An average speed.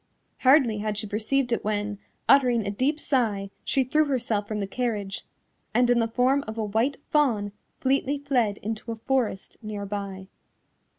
Yes: average, 170 wpm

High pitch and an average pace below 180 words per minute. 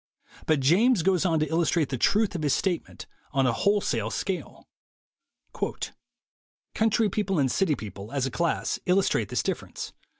No: medium, 170 Hz; average, 165 wpm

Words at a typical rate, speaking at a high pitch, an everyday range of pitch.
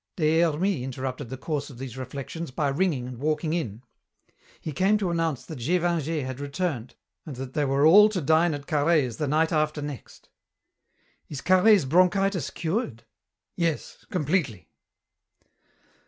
No: average, 150 wpm; medium, 155 Hz; average, 4.3 semitones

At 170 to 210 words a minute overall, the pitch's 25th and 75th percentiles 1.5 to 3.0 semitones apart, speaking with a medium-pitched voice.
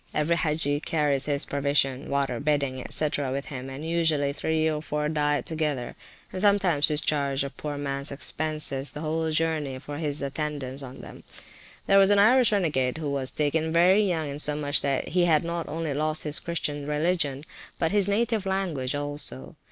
Yes: average, 175 wpm; narrow, 2.5 semitones; medium, 150 Hz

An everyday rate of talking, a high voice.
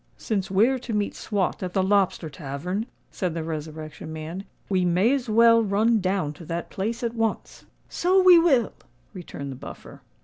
Yes: average, 175 wpm; high, 195 Hz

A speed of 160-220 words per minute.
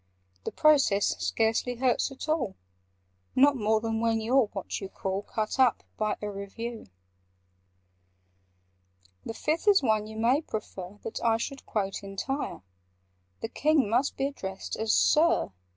No: average, 150 wpm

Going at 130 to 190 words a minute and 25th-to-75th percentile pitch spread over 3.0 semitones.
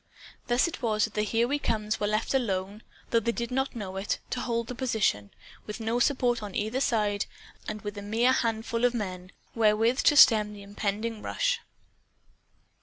No: average, 185 wpm; narrow, 2.5 semitones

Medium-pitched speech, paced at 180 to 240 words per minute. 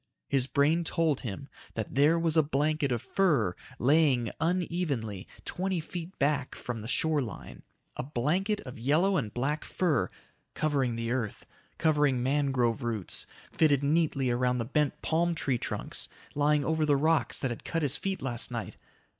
No: medium, 145 Hz; average, 165 wpm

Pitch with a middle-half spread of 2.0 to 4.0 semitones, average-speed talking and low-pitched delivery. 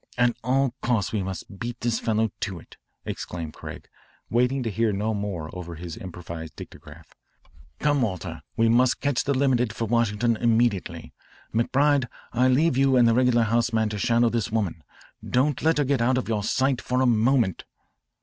Yes: average, 3.6 semitones; average, 180 wpm; low, 115 Hz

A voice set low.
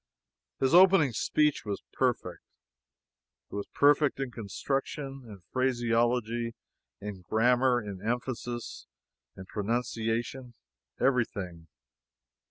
Yes: low, 120 Hz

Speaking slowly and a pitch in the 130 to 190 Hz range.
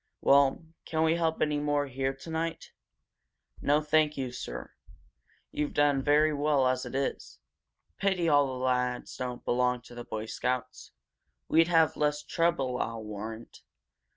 No: average, 150 wpm; medium, 140 Hz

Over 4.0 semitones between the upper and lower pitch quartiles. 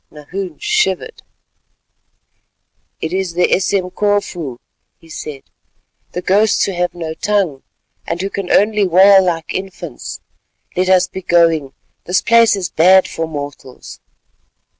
No: average, 3.2 semitones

